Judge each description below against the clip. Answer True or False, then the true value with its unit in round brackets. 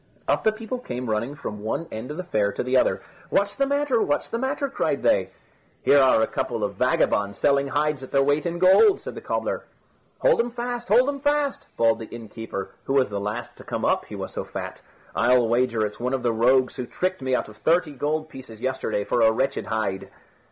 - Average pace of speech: False (230 wpm)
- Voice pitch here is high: False (135 Hz)